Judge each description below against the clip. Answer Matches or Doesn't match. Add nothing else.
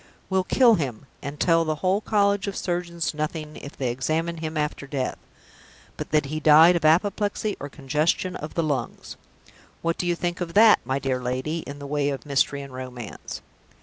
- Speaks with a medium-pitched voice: Matches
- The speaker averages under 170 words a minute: Doesn't match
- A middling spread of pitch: Matches